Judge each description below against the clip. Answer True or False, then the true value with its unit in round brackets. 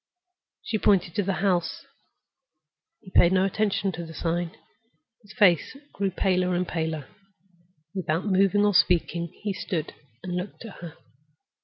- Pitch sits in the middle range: True (180 Hz)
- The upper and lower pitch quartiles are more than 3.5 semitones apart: False (2.5 semitones)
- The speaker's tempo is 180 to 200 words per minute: False (145 wpm)